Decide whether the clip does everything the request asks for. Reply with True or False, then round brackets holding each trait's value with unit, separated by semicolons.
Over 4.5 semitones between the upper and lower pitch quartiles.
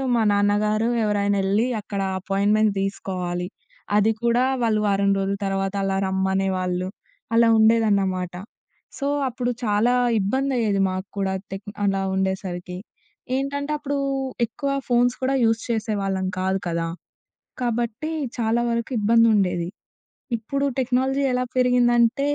False (3.7 semitones)